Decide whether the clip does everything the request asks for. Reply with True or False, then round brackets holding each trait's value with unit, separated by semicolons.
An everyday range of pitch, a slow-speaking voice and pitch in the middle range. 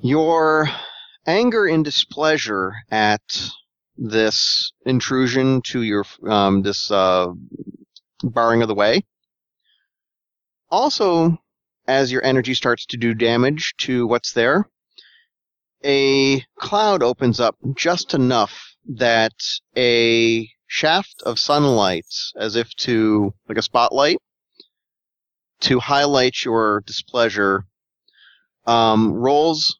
False (4.4 semitones; 100 wpm; 120 Hz)